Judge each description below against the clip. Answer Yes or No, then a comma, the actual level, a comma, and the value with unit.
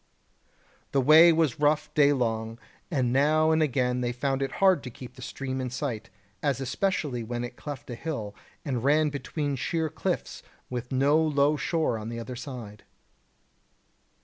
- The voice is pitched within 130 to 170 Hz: Yes, low, 135 Hz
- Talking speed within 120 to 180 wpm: Yes, average, 165 wpm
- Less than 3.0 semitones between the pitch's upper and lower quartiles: No, average, 3.8 semitones